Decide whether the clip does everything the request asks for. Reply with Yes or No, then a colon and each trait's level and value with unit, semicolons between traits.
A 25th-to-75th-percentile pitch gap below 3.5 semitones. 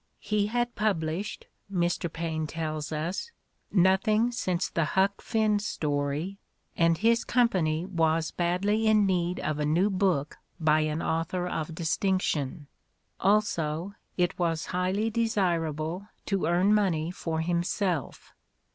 No: average, 3.9 semitones